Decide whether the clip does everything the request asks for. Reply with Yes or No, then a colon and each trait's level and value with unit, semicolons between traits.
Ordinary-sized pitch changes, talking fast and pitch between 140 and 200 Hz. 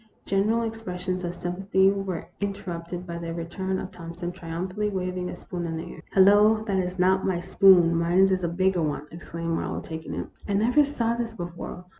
No: narrow, 2.3 semitones; fast, 210 wpm; medium, 185 Hz